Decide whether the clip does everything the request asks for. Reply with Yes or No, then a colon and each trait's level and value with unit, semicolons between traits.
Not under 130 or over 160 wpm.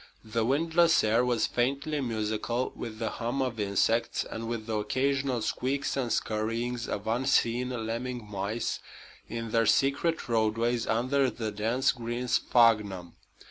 Yes: average, 140 wpm